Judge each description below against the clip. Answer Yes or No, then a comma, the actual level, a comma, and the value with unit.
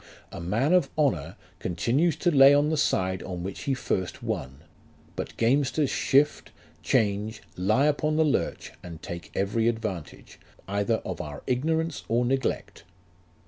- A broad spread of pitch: Yes, wide, 7.5 semitones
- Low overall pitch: Yes, low, 115 Hz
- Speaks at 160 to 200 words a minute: No, average, 145 wpm